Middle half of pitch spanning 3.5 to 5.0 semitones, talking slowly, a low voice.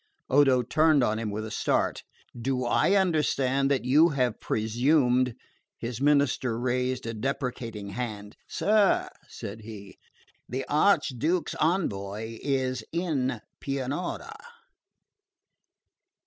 Yes: average, 4.1 semitones; slow, 110 wpm; low, 130 Hz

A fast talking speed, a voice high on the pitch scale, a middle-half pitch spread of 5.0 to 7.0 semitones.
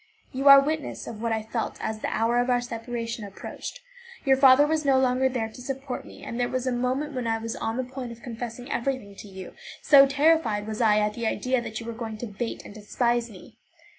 No: fast, 235 wpm; high, 240 Hz; average, 2.8 semitones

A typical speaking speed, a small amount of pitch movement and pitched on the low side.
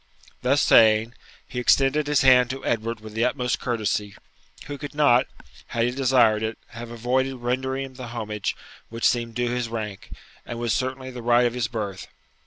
Yes: average, 190 wpm; narrow, 2.3 semitones; low, 120 Hz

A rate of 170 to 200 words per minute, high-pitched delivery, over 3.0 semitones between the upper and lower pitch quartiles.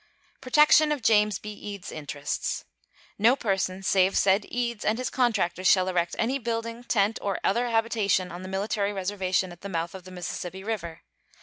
Yes: average, 175 wpm; high, 200 Hz; average, 3.6 semitones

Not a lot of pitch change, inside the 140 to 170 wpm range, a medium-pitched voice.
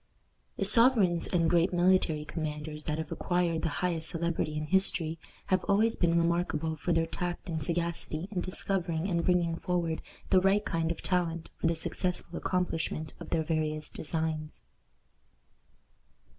Yes: narrow, 2.0 semitones; average, 150 wpm; medium, 170 Hz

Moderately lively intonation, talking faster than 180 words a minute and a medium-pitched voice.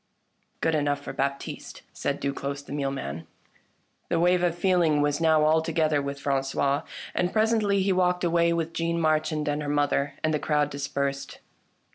No: average, 3.1 semitones; average, 175 wpm; medium, 155 Hz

